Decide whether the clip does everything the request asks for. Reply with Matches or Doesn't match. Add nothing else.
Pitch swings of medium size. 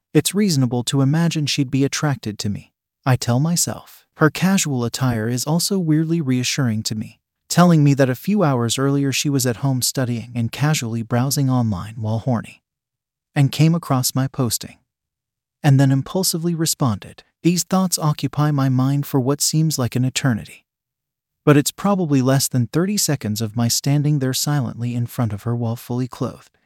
Matches